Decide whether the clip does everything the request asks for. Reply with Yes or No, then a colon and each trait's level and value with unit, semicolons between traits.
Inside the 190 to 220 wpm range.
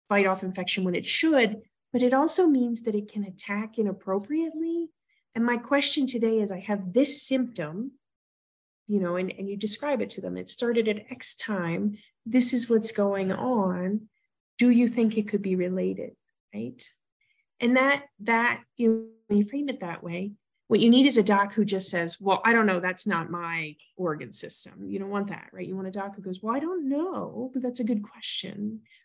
Yes: fast, 205 wpm